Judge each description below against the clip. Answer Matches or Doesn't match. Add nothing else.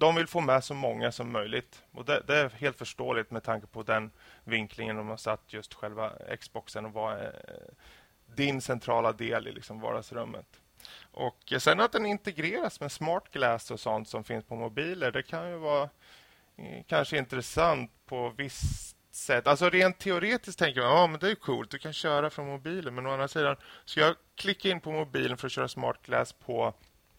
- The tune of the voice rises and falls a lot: Matches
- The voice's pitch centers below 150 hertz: Matches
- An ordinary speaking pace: Matches